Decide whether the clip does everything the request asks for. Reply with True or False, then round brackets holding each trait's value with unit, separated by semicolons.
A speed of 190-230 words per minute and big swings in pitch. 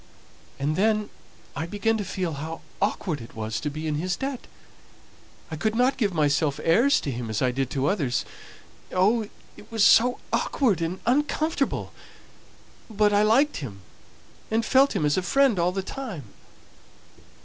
False (160 wpm; 7.1 semitones)